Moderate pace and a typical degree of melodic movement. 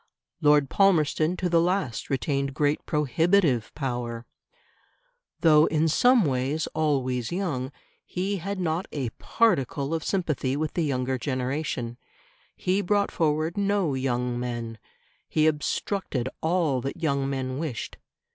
No: slow, 130 wpm; average, 4.7 semitones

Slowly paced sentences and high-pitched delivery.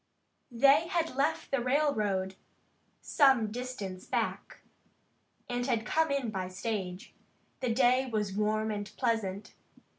Yes: slow, 120 wpm; high, 230 Hz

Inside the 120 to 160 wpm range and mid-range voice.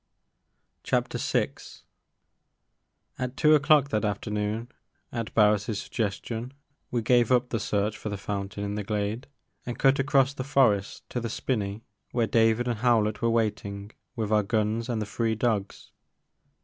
No: average, 155 wpm; low, 110 Hz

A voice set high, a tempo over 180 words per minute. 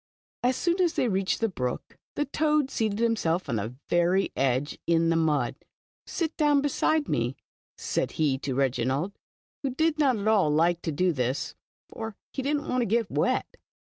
Yes: high, 195 Hz; average, 190 wpm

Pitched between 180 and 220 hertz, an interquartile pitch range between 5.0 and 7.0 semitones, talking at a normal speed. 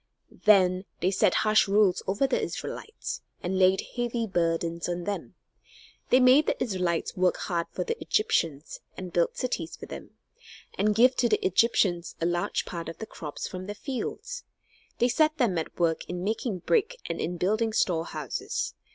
Yes: high, 190 Hz; wide, 5.4 semitones; average, 170 wpm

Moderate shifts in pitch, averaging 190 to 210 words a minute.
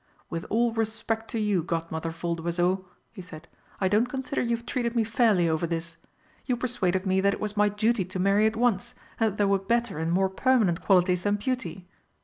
Yes: average, 4.2 semitones; average, 200 wpm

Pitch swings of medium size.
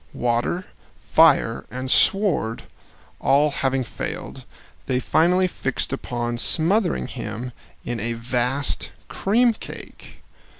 No: wide, 6.2 semitones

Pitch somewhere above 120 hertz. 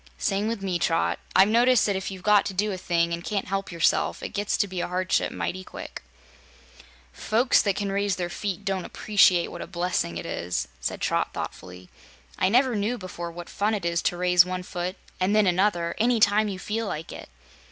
Yes: high, 190 Hz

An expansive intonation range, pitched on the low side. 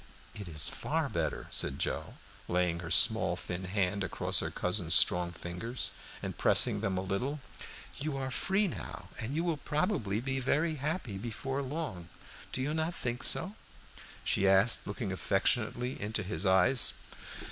Yes: wide, 6.8 semitones; low, 110 Hz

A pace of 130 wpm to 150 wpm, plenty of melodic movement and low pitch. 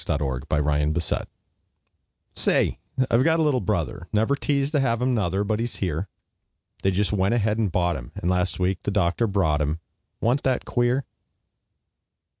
No: average, 170 wpm; wide, 5.8 semitones; low, 100 Hz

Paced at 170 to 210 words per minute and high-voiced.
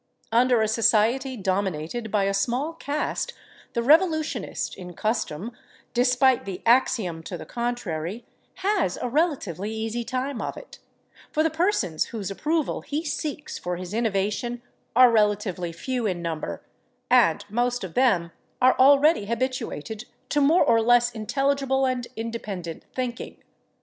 No: average, 140 wpm; high, 235 Hz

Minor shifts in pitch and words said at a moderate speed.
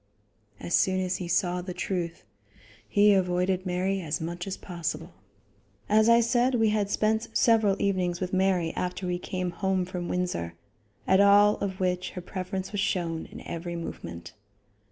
Yes: narrow, 2.1 semitones; average, 165 wpm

